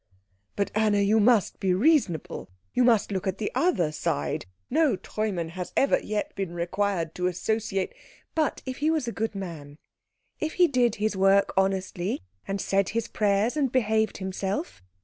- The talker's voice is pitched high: Yes, high, 200 Hz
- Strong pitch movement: No, average, 3.7 semitones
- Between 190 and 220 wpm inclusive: No, average, 170 wpm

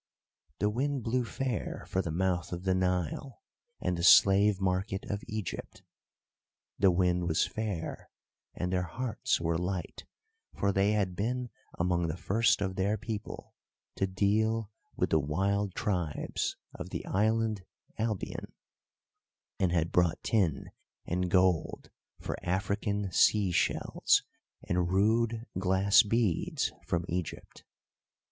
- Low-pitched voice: Yes, very low, 95 Hz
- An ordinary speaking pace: No, slow, 130 wpm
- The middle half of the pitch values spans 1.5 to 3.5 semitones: Yes, average, 3.1 semitones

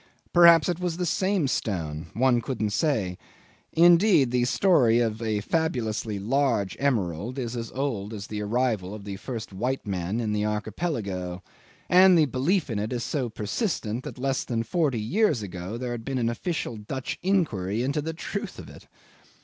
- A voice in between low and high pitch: No, low, 120 Hz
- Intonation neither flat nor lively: No, wide, 6.0 semitones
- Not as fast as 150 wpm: No, average, 175 wpm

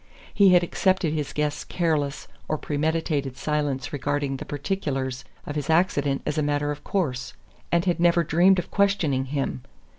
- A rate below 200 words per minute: Yes, average, 160 wpm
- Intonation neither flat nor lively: Yes, average, 3.4 semitones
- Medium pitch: Yes, medium, 150 Hz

